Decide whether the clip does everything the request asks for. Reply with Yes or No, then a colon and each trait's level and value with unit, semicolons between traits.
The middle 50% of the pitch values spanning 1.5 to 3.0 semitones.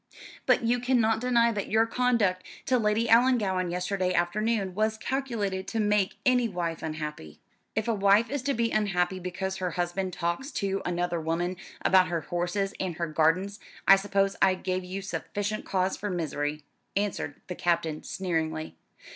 No: average, 3.7 semitones